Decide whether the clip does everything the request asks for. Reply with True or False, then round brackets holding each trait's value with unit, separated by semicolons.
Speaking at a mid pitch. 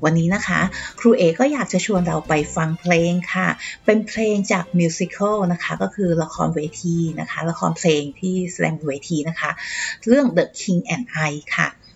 True (175 Hz)